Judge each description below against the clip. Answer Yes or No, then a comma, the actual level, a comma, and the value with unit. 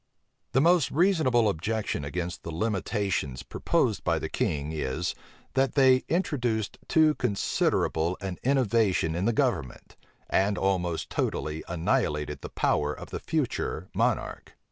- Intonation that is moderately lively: No, wide, 7.8 semitones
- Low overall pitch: Yes, low, 100 Hz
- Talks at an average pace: No, slow, 130 wpm